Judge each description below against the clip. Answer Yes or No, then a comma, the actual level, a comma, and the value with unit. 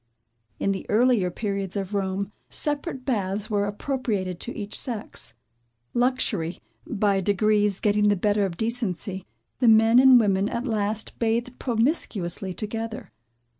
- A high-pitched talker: Yes, high, 210 Hz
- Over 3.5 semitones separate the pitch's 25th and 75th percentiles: No, average, 3.0 semitones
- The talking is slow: Yes, slow, 130 wpm